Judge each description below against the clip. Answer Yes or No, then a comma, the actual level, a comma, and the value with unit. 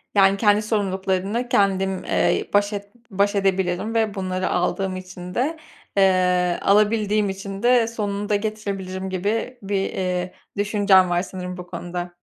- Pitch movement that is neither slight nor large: No, narrow, 2.0 semitones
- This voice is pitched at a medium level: No, high, 195 Hz